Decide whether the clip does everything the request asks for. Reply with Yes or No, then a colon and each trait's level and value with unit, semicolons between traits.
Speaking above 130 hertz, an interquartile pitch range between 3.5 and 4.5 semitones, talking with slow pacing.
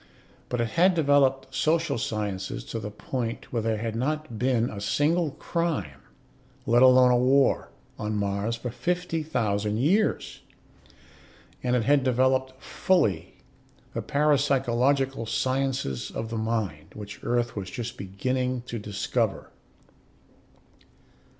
No: low, 125 Hz; average, 4.0 semitones; slow, 125 wpm